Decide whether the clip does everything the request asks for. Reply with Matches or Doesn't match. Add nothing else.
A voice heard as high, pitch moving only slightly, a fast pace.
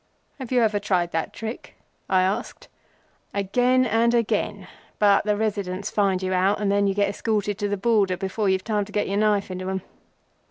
Doesn't match